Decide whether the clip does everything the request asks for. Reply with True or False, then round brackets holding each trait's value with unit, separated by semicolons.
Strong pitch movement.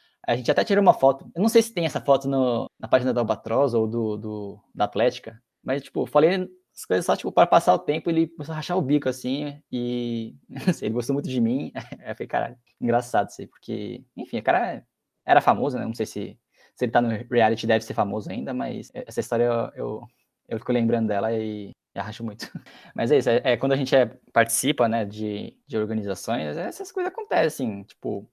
False (4.0 semitones)